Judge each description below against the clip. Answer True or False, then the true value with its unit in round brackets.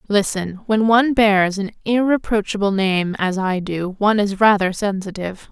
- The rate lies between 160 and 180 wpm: False (140 wpm)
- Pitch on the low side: False (205 Hz)